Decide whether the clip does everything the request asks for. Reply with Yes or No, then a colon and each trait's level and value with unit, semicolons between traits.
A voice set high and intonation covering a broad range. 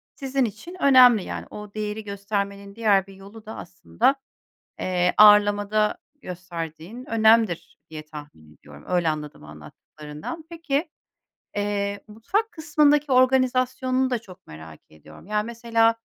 Yes: high, 210 Hz; wide, 5.9 semitones